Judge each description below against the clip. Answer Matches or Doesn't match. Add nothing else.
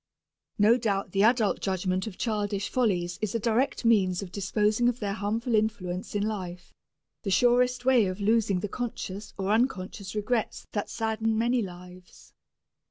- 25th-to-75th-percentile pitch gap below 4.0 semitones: Matches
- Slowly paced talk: Doesn't match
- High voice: Matches